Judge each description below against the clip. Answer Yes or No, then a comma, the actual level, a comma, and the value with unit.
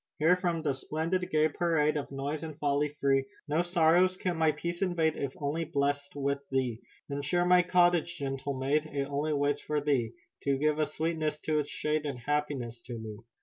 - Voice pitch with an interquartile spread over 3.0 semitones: No, narrow, 2.6 semitones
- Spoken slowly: No, average, 195 wpm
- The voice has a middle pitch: Yes, medium, 150 Hz